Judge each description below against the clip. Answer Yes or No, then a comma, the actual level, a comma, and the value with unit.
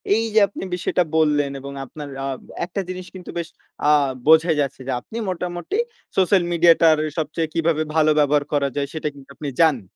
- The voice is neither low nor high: Yes, medium, 160 Hz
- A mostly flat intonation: No, average, 3.3 semitones